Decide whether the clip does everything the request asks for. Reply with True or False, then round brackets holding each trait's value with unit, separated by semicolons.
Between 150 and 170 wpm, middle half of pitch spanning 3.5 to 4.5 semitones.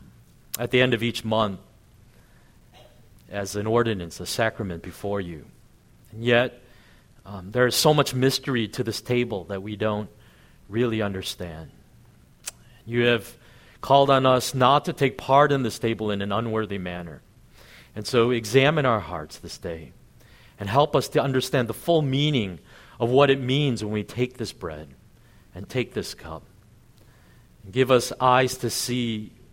True (160 wpm; 3.8 semitones)